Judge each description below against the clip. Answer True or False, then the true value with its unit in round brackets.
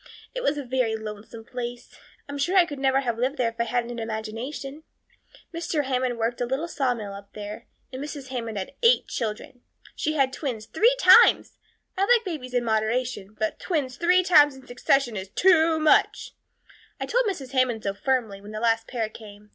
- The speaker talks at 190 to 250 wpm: True (195 wpm)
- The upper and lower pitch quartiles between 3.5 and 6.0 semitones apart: True (4.6 semitones)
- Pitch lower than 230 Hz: False (250 Hz)